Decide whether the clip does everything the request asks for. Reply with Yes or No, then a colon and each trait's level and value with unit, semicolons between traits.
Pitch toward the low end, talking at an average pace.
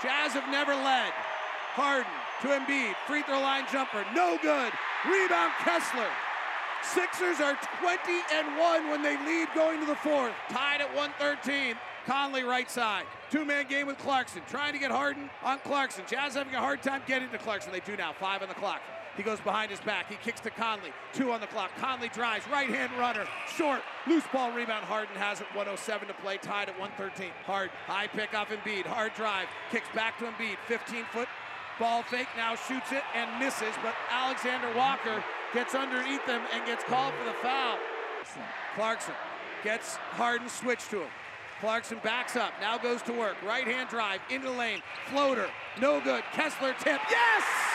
No: very high, 250 Hz; average, 180 wpm